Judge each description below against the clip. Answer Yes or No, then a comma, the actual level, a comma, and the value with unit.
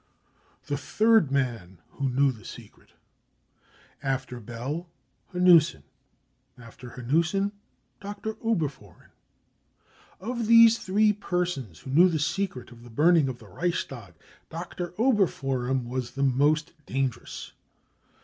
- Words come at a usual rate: No, slow, 110 wpm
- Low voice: No, medium, 145 Hz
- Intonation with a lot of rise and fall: Yes, wide, 6.6 semitones